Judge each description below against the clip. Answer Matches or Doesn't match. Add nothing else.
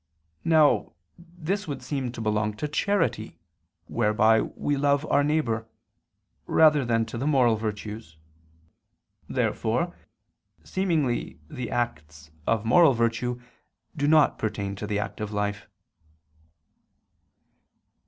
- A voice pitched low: Matches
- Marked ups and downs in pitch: Matches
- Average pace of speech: Doesn't match